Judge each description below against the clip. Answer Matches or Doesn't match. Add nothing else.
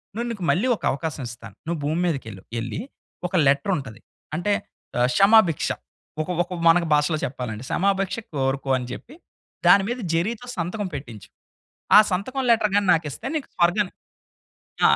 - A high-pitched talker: Doesn't match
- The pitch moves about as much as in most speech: Doesn't match